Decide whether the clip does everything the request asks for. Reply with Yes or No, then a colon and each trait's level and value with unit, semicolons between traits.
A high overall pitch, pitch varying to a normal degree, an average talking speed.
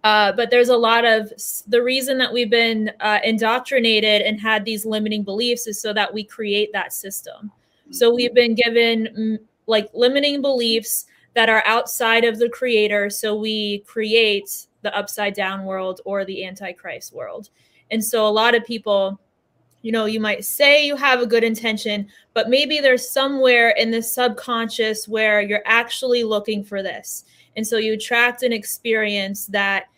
No: high, 220 Hz; narrow, 2.1 semitones; average, 170 wpm